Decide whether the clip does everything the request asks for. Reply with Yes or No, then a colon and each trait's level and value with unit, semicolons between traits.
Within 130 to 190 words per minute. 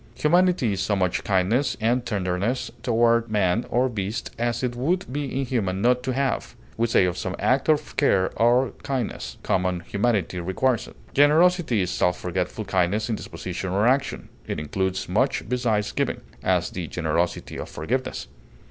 Yes: average, 165 wpm